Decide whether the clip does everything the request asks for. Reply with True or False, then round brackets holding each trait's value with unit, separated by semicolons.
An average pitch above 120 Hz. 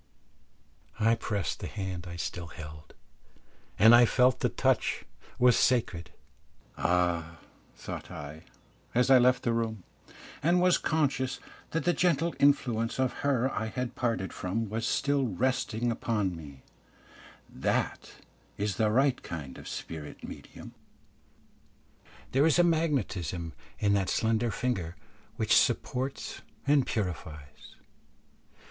False (115 Hz)